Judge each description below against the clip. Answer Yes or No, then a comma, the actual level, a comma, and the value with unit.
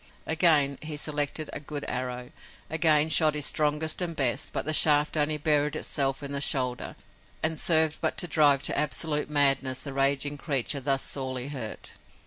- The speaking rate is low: No, average, 170 wpm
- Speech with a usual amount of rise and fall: No, narrow, 2.1 semitones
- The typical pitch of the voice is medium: Yes, medium, 145 Hz